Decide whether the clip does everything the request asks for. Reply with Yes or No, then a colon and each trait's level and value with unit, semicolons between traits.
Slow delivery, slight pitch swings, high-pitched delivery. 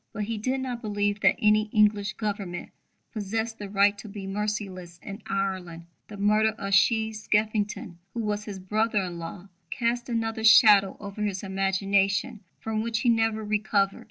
No: average, 165 wpm; narrow, 1.9 semitones; high, 210 Hz